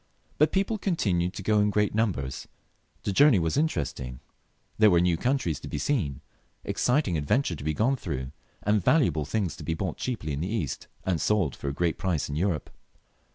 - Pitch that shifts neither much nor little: No, wide, 6.3 semitones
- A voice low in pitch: Yes, very low, 95 Hz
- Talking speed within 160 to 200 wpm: Yes, average, 195 wpm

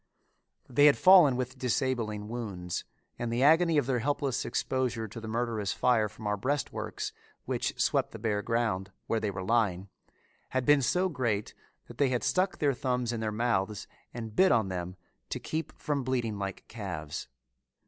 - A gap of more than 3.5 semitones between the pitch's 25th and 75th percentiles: Yes, average, 4.0 semitones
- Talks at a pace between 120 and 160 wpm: No, average, 175 wpm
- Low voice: Yes, low, 120 Hz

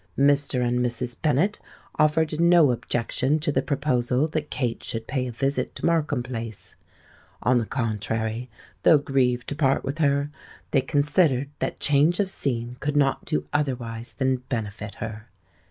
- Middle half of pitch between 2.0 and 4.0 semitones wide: Yes, average, 3.4 semitones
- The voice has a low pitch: Yes, low, 130 Hz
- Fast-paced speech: No, average, 155 wpm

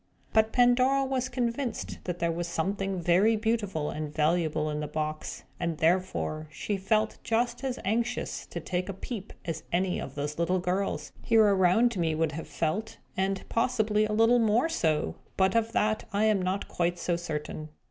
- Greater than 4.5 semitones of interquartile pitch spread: Yes, average, 5.0 semitones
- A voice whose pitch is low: No, high, 190 Hz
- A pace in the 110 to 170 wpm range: No, average, 180 wpm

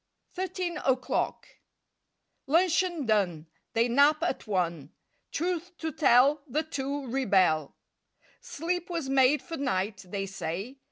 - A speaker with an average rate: No, slow, 125 wpm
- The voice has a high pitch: Yes, very high, 270 Hz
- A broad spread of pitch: Yes, wide, 8.5 semitones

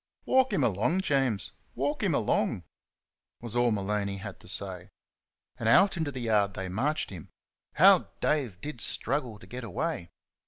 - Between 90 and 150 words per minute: No, average, 160 wpm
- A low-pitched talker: Yes, low, 115 Hz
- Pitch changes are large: Yes, wide, 6.3 semitones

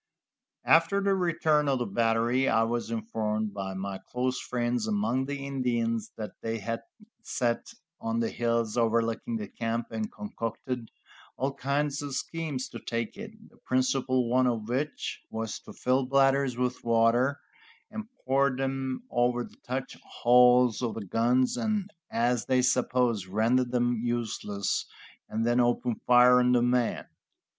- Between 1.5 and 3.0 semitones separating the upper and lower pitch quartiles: Yes, average, 2.7 semitones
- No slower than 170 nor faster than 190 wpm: No, average, 150 wpm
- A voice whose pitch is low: Yes, low, 125 Hz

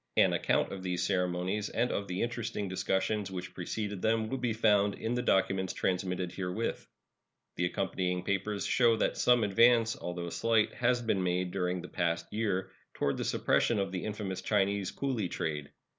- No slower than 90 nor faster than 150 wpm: No, average, 175 wpm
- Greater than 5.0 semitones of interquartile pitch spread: No, average, 3.4 semitones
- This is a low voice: Yes, very low, 95 Hz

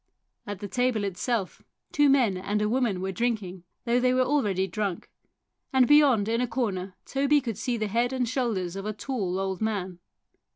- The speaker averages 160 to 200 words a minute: Yes, average, 190 wpm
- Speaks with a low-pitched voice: No, high, 220 Hz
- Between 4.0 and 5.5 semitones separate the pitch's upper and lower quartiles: Yes, average, 4.6 semitones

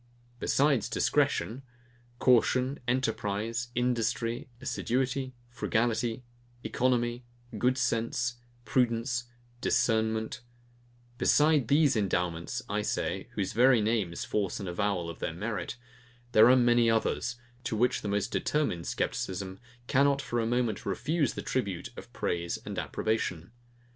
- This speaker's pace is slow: Yes, slow, 120 wpm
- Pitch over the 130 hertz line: No, low, 115 Hz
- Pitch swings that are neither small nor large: Yes, average, 3.4 semitones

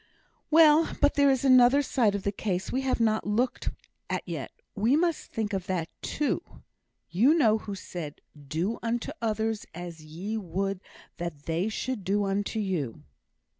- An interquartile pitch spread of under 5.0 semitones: No, wide, 5.4 semitones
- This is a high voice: Yes, high, 210 Hz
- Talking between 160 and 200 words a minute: Yes, average, 165 wpm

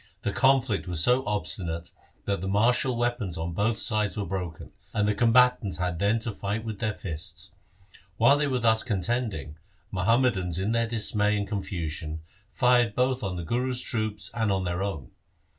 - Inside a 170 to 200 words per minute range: Yes, average, 175 wpm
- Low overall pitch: Yes, low, 105 Hz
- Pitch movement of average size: Yes, average, 4.4 semitones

